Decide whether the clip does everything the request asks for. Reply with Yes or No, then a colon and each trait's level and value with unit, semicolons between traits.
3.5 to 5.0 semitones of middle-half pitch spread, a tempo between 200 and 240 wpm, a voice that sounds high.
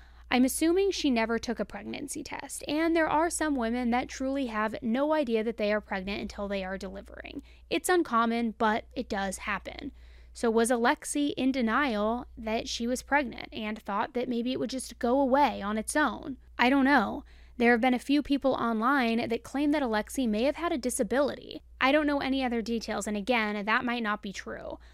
Yes: average, 4.3 semitones; fast, 205 wpm; high, 245 Hz